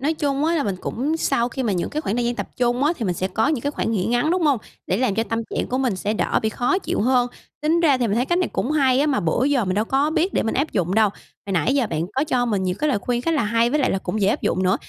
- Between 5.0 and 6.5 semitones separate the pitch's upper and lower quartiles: Yes, average, 5.3 semitones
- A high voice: Yes, high, 245 Hz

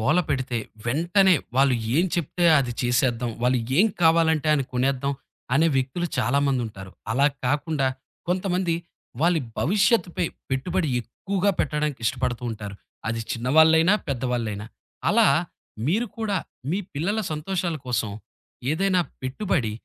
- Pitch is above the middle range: No, medium, 145 Hz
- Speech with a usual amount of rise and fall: No, wide, 5.9 semitones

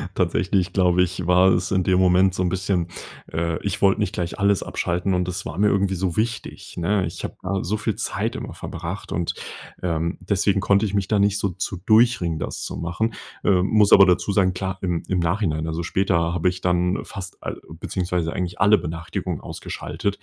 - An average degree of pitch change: No, narrow, 2.1 semitones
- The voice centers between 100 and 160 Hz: No, very low, 90 Hz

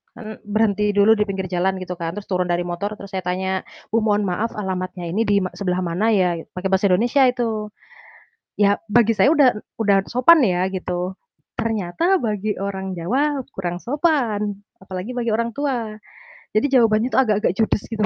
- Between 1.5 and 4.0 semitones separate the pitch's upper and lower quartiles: Yes, average, 3.6 semitones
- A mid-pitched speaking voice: No, high, 205 Hz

